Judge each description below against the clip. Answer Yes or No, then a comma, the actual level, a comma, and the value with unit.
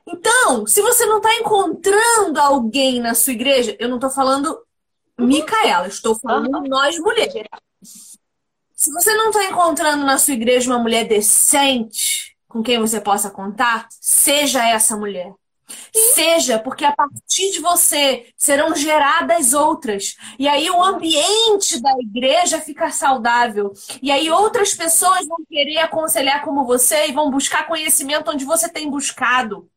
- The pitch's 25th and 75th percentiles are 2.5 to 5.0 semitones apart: No, wide, 5.4 semitones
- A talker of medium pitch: No, very high, 290 Hz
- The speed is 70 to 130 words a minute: No, average, 145 wpm